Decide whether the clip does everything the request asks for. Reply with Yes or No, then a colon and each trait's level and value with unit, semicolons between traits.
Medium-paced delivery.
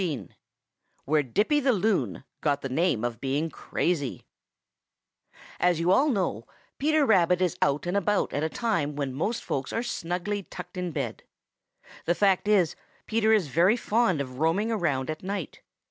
Yes: average, 165 wpm